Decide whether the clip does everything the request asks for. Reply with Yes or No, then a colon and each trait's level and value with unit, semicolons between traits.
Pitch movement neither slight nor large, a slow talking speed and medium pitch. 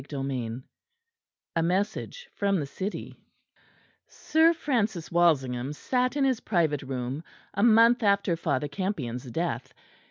No: wide, 8.1 semitones; slow, 125 wpm; medium, 175 Hz